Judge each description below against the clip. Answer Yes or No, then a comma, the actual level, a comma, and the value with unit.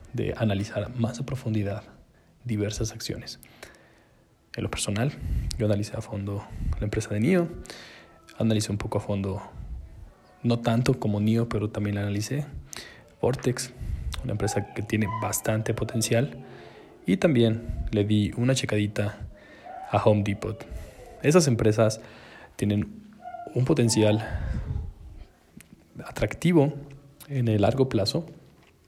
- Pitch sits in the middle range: No, low, 110 Hz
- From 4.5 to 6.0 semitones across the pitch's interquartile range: No, average, 2.7 semitones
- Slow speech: Yes, slow, 120 wpm